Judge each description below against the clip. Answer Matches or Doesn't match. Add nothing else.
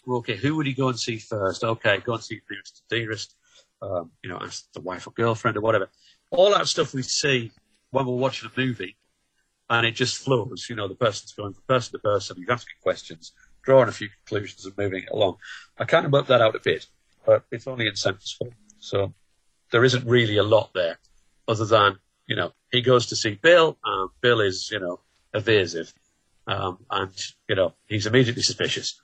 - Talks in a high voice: Doesn't match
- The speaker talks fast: Matches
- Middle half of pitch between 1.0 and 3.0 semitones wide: Doesn't match